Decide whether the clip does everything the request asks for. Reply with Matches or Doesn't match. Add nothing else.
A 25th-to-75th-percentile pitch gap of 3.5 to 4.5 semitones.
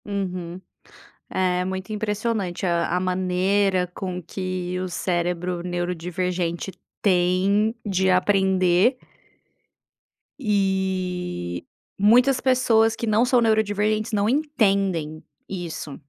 Doesn't match